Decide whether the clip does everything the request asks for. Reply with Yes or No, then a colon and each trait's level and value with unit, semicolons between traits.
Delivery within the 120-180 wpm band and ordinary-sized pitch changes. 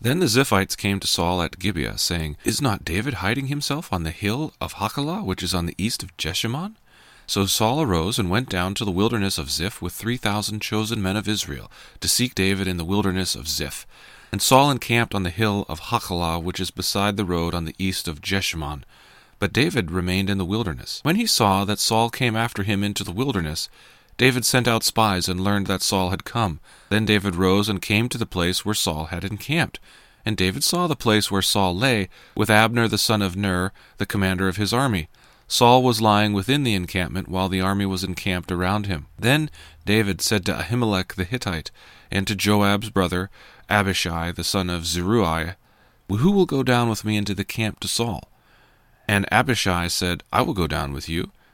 No: fast, 205 wpm; average, 3.6 semitones